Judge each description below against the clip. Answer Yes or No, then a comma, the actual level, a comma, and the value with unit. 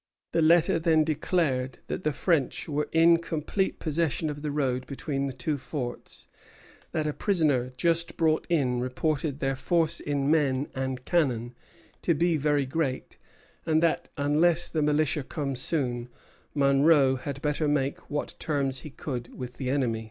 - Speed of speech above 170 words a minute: No, average, 160 wpm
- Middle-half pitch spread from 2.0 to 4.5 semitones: Yes, average, 3.3 semitones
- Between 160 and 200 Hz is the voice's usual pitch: No, medium, 145 Hz